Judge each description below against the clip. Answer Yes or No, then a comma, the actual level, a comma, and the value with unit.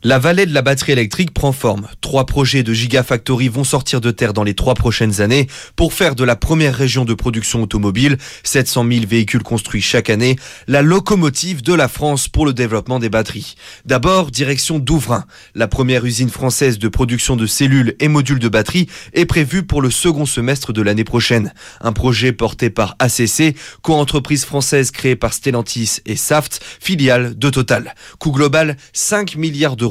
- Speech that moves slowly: No, average, 180 wpm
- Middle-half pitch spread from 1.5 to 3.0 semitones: No, average, 3.8 semitones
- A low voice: Yes, low, 130 Hz